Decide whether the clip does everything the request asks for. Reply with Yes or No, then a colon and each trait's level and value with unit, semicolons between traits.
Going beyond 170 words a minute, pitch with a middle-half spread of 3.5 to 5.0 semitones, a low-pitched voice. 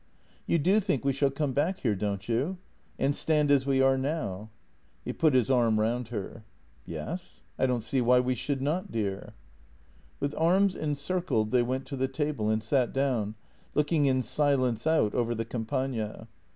Yes: average, 180 wpm; average, 4.3 semitones; low, 130 Hz